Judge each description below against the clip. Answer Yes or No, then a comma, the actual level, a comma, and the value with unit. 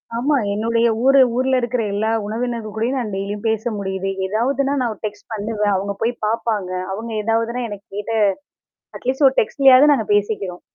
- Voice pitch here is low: No, high, 225 Hz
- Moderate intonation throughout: Yes, average, 3.3 semitones